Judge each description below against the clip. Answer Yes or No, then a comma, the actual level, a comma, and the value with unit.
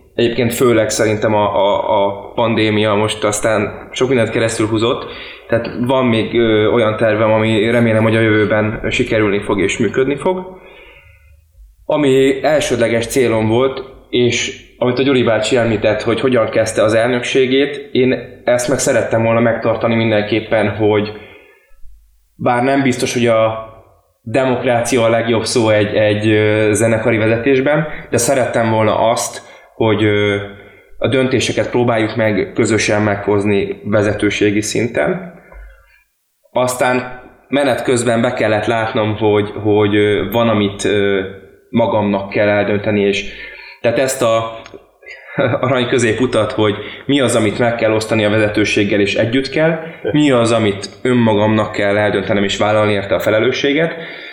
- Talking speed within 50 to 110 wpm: No, average, 135 wpm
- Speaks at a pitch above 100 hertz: Yes, low, 110 Hz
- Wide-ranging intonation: No, narrow, 2.6 semitones